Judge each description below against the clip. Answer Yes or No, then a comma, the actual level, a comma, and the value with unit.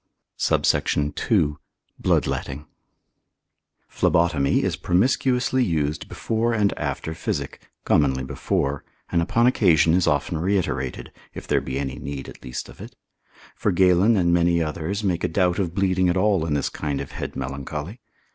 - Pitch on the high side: No, very low, 85 Hz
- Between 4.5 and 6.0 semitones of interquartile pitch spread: Yes, average, 4.8 semitones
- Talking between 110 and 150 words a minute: Yes, average, 145 wpm